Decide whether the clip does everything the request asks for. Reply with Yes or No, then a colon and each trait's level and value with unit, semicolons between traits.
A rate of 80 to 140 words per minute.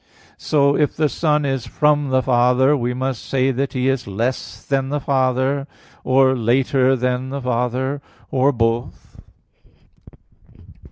Yes: slow, 135 wpm